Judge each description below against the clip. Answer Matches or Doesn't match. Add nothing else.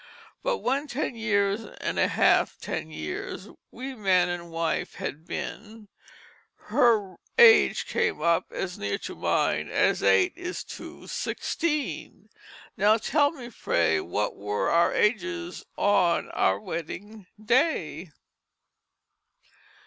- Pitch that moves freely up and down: Matches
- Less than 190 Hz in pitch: Doesn't match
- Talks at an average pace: Doesn't match